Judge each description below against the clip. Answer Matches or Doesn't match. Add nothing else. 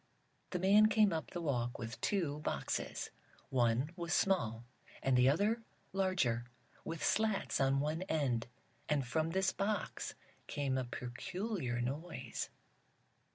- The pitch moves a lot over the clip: Matches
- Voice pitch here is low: Doesn't match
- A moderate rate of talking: Doesn't match